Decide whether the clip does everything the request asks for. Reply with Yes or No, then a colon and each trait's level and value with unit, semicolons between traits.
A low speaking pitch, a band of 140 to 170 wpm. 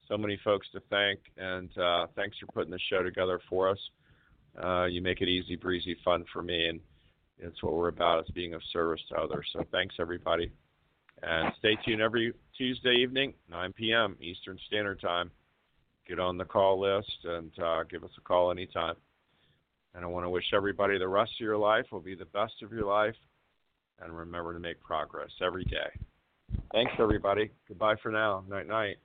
No: very low, 95 Hz; average, 190 wpm